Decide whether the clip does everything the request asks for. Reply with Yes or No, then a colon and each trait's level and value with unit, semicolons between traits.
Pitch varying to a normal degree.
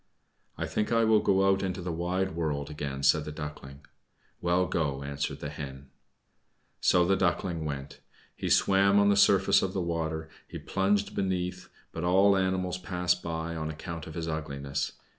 Yes: average, 4.0 semitones